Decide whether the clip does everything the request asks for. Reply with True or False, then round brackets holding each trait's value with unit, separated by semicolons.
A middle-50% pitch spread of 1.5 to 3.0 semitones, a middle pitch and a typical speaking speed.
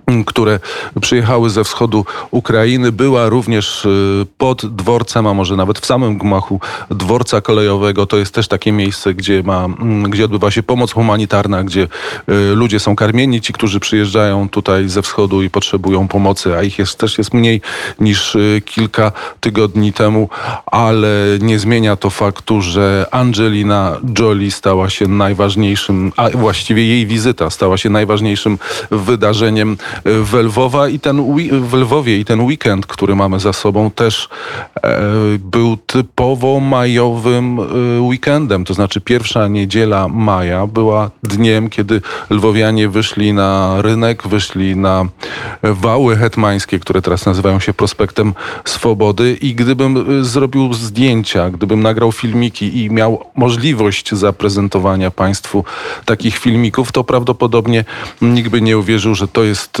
False (2.7 semitones; 110 Hz; 135 wpm)